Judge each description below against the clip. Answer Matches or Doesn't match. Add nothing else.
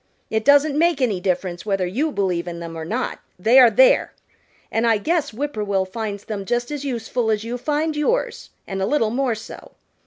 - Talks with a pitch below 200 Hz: Doesn't match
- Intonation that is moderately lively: Doesn't match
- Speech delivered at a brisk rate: Matches